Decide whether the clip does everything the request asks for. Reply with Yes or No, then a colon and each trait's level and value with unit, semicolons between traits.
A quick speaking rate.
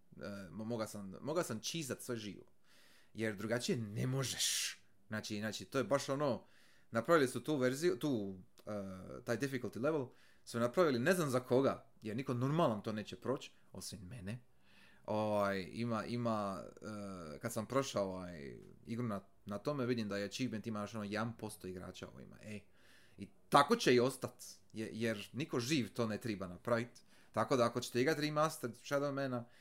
Yes: fast, 170 wpm